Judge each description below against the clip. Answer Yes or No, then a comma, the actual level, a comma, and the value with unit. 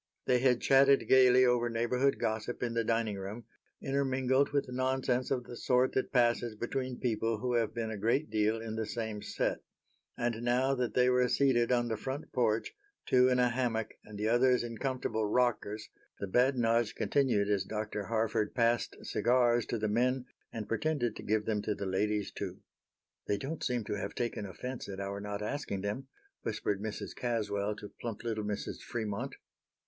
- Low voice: Yes, low, 120 Hz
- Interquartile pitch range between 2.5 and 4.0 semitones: Yes, average, 2.9 semitones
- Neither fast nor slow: Yes, average, 185 wpm